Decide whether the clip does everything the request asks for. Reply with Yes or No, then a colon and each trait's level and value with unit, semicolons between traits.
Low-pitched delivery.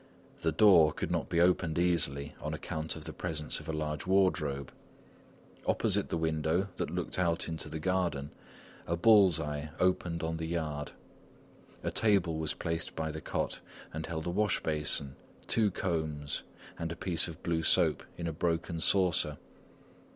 Yes: very low, 80 Hz